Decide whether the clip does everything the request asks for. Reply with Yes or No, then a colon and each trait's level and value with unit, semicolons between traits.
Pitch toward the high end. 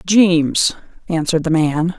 No: medium, 165 Hz